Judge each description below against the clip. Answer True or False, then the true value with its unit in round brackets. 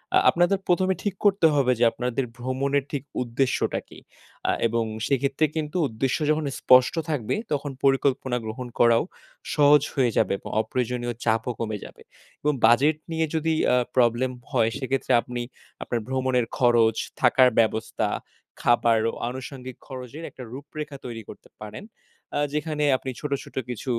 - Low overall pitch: True (130 Hz)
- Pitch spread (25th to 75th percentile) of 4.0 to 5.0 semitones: False (3.3 semitones)